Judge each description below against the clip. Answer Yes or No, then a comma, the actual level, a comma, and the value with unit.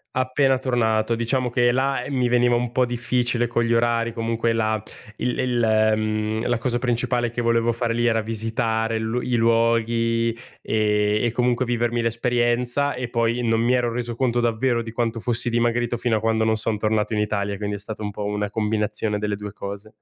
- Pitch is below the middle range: Yes, low, 115 Hz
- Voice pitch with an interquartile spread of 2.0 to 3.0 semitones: No, narrow, 1.6 semitones